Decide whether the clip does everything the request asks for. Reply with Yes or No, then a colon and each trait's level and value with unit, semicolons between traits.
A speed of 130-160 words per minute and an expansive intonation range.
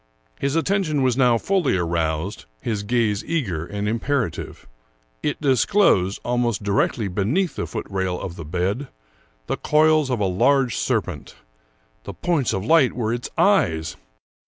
Yes: average, 155 wpm; wide, 7.1 semitones